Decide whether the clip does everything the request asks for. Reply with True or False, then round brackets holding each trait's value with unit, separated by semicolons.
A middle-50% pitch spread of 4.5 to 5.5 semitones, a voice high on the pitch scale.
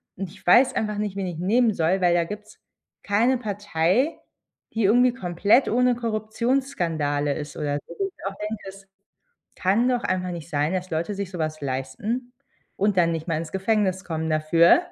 True (4.9 semitones; 195 Hz)